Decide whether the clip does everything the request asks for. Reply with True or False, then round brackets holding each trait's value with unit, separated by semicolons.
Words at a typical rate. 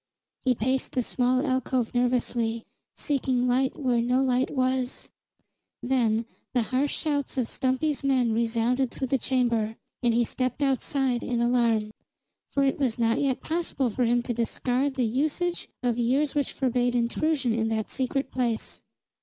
True (155 wpm)